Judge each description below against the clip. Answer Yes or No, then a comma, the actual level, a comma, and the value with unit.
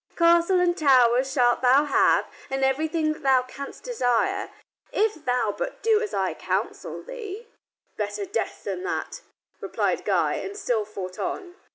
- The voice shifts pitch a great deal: Yes, wide, 7.5 semitones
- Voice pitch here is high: Yes, very high, 315 Hz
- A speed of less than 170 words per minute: Yes, average, 155 wpm